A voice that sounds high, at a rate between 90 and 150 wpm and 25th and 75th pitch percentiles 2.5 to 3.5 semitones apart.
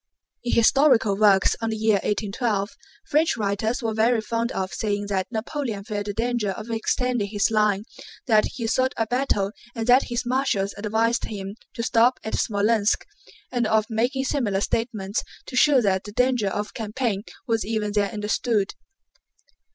No: high, 220 Hz; average, 165 wpm; average, 2.9 semitones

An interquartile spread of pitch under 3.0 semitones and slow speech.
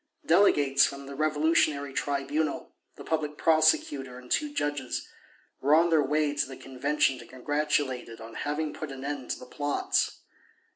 No: narrow, 2.4 semitones; average, 160 wpm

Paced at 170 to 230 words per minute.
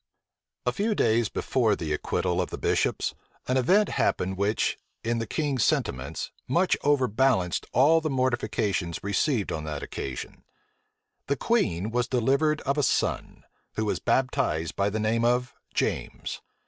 No: average, 150 wpm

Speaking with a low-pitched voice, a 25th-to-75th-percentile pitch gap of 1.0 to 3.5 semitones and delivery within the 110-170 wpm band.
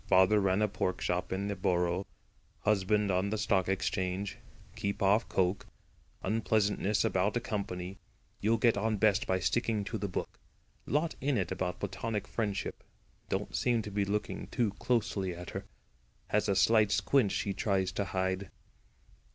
Yes: low, 100 Hz; narrow, 2.4 semitones; average, 160 wpm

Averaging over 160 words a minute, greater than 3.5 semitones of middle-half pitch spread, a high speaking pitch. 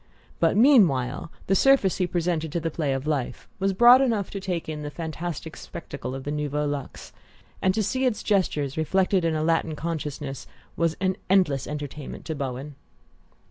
No: average, 180 wpm; average, 4.6 semitones; medium, 160 Hz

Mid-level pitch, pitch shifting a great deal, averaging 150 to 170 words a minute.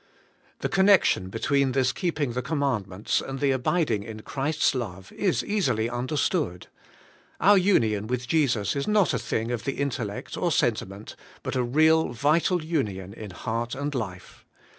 No: low, 130 Hz; wide, 5.9 semitones; average, 165 wpm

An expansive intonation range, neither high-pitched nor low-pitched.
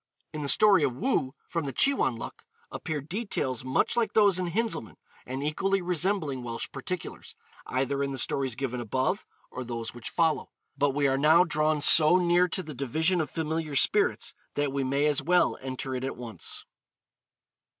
No: average, 4.8 semitones; medium, 145 Hz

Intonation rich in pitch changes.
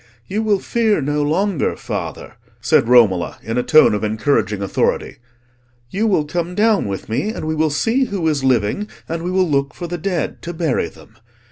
Yes: wide, 7.5 semitones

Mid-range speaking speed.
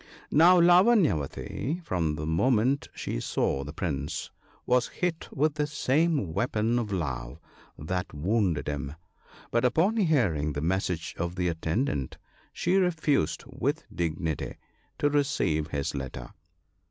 No: slow, 130 wpm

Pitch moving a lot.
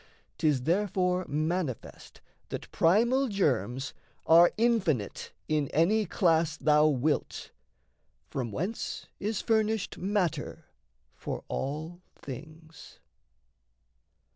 No: average, 5.0 semitones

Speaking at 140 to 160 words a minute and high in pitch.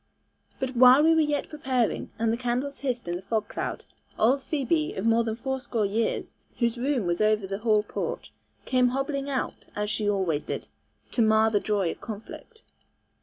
No: average, 190 wpm; high, 235 Hz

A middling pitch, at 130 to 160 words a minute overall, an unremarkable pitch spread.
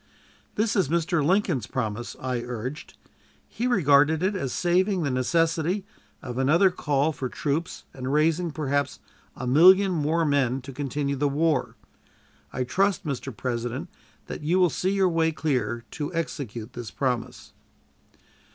Yes: medium, 150 Hz; average, 145 wpm; average, 4.9 semitones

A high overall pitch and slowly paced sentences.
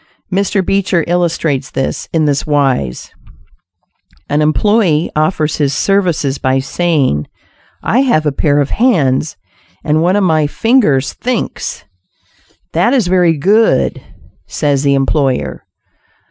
No: medium, 155 Hz; slow, 120 wpm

